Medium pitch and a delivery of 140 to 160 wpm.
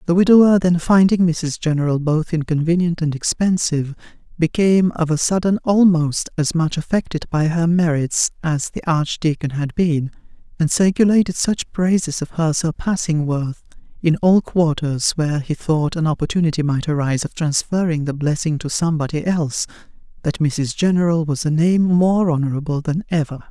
Yes: medium, 160 Hz; average, 155 wpm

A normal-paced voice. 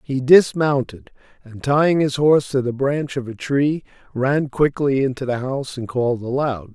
Yes: average, 180 wpm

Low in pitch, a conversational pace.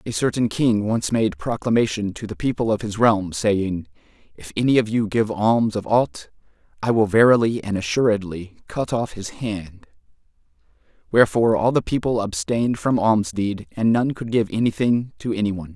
Yes: low, 110 Hz; average, 175 wpm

